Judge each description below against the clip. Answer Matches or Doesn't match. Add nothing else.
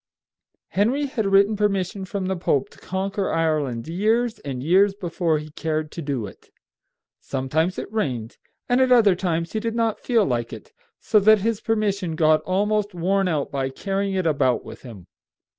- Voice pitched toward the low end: Doesn't match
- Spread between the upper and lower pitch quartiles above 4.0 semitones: Matches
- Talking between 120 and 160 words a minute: Doesn't match